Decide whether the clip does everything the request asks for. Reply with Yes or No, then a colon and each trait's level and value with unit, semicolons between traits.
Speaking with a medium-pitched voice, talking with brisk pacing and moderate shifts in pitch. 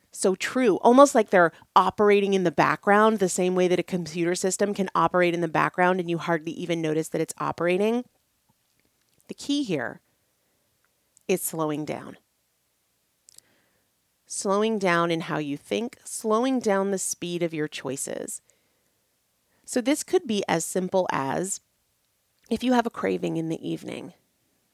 No: medium, 180 Hz; average, 155 wpm; average, 4.1 semitones